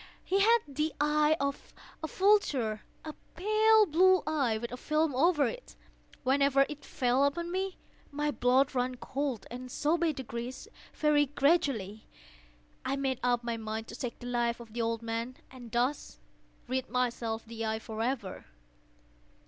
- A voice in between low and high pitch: No, very high, 260 Hz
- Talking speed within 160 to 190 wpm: No, average, 150 wpm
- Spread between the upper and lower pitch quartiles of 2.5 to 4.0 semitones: No, average, 4.5 semitones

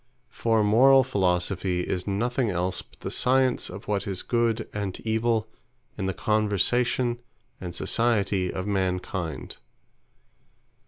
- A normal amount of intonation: Yes, average, 4.1 semitones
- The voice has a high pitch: No, low, 105 Hz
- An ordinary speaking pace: No, slow, 120 wpm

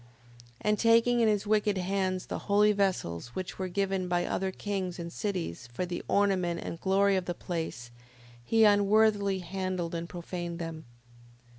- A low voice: No, high, 190 Hz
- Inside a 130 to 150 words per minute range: No, average, 170 wpm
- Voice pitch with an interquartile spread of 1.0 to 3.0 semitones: Yes, average, 2.7 semitones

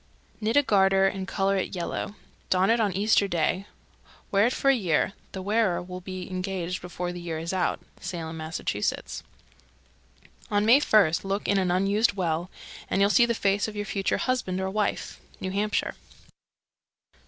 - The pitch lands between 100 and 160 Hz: No, high, 195 Hz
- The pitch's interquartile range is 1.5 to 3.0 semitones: Yes, narrow, 2.4 semitones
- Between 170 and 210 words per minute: Yes, average, 175 wpm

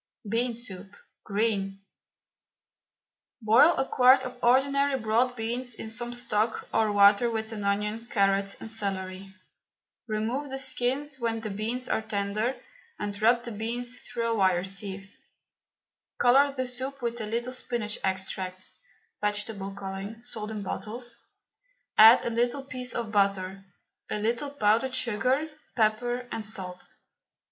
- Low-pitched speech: No, high, 225 Hz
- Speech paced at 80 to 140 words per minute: Yes, slow, 135 wpm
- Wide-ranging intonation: No, average, 3.3 semitones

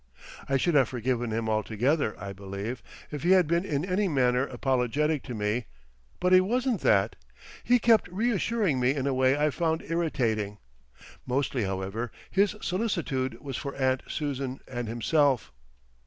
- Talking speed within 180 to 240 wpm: No, average, 155 wpm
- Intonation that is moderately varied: No, wide, 6.3 semitones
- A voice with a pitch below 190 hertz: Yes, low, 135 Hz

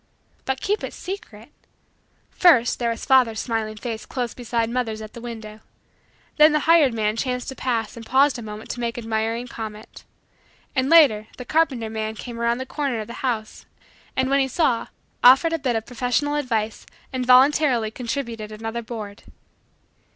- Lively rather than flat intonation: No, average, 3.1 semitones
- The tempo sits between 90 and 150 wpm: No, average, 175 wpm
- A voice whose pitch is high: Yes, high, 235 Hz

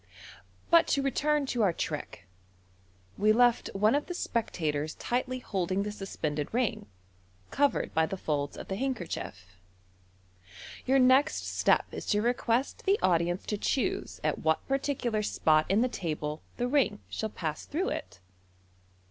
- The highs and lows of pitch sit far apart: Yes, wide, 8.1 semitones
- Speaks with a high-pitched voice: Yes, high, 215 Hz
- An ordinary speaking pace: Yes, average, 150 wpm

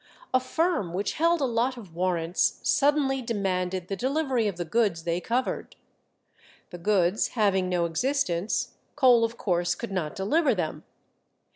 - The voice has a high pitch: Yes, high, 205 Hz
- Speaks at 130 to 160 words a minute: Yes, average, 150 wpm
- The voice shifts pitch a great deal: Yes, wide, 6.4 semitones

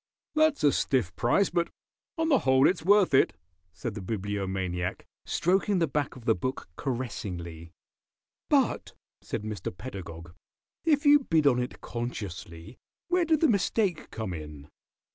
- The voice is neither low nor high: No, low, 125 Hz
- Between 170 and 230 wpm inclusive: No, average, 145 wpm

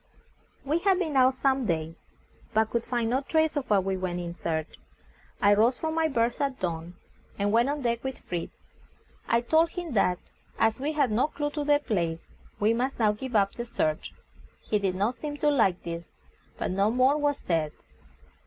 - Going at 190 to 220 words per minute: Yes, average, 200 wpm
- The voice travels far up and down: Yes, wide, 6.9 semitones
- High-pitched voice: Yes, high, 235 Hz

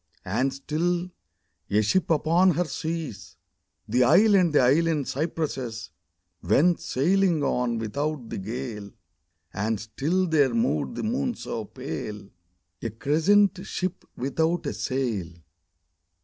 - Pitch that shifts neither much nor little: No, wide, 7.1 semitones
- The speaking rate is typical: No, slow, 120 wpm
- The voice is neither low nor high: Yes, medium, 145 Hz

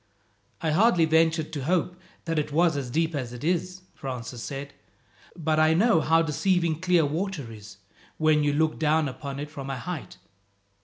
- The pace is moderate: Yes, average, 175 wpm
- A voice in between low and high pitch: Yes, medium, 155 Hz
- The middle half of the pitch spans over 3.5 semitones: No, average, 2.8 semitones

